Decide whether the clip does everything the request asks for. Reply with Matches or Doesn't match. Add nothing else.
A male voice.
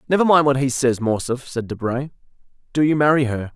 Matches